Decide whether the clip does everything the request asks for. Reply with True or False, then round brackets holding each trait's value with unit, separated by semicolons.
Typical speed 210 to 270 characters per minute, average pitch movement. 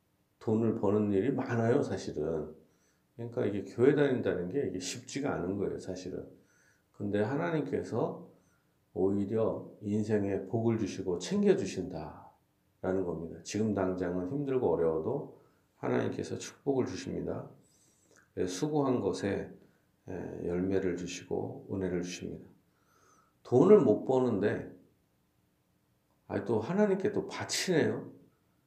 True (265 characters per minute; 4.2 semitones)